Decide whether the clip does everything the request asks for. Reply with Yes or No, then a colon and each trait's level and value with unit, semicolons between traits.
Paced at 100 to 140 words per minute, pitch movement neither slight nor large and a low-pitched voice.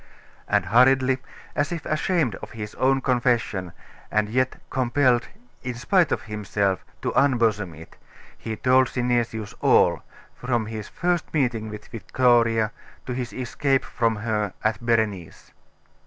Yes: slow, 135 wpm; average, 3.2 semitones; low, 120 Hz